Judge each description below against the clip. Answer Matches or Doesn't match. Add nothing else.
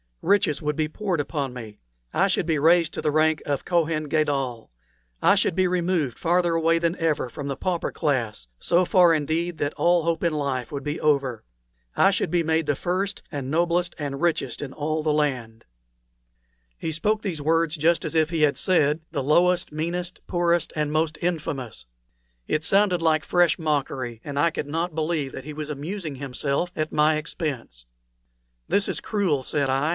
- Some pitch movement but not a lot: Matches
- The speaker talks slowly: Doesn't match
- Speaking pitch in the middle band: Matches